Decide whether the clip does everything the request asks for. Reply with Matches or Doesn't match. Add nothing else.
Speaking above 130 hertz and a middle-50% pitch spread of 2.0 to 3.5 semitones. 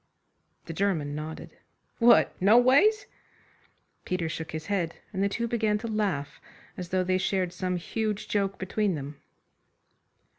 Doesn't match